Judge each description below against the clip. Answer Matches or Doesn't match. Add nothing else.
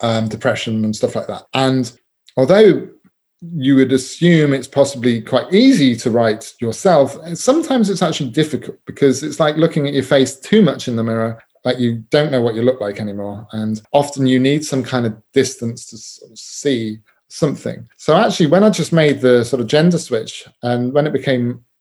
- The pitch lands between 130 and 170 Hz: Matches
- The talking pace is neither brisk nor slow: Matches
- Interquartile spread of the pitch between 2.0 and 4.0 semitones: Doesn't match